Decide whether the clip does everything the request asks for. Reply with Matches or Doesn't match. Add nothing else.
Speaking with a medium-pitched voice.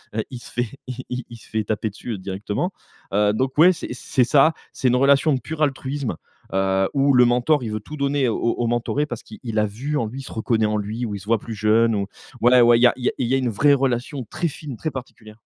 Doesn't match